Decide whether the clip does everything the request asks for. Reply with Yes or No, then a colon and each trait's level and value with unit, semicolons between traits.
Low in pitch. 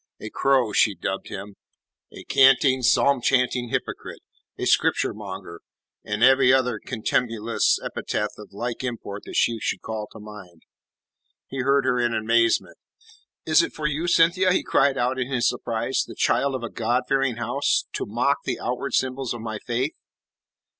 Yes: low, 120 Hz